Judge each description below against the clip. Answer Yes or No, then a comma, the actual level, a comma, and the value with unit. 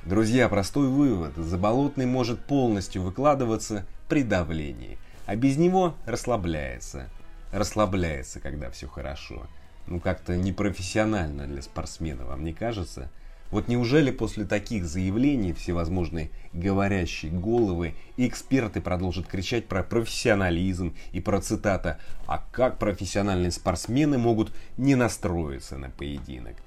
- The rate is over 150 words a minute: No, slow, 110 wpm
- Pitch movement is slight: No, average, 5.3 semitones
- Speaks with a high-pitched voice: No, very low, 95 Hz